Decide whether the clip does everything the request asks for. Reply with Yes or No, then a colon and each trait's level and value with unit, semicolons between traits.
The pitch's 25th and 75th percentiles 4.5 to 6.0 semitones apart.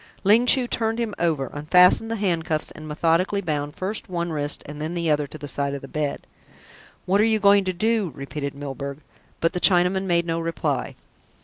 Yes: average, 4.9 semitones